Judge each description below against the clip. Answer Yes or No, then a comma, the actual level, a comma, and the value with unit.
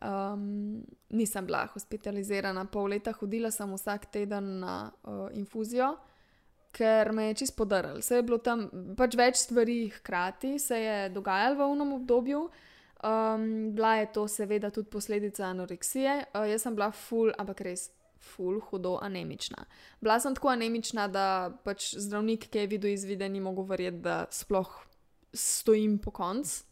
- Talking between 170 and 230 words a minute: No, average, 155 wpm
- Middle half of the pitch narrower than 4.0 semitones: Yes, narrow, 2.5 semitones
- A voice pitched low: No, high, 210 Hz